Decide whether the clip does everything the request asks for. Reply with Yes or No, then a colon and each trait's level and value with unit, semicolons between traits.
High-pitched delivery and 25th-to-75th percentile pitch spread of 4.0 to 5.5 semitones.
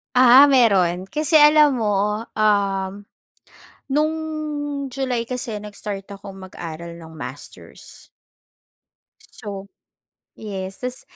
Yes: high, 210 Hz; average, 4.7 semitones